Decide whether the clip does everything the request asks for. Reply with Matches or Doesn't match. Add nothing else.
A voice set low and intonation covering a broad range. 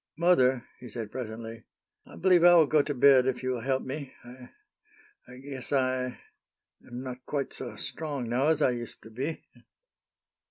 Doesn't match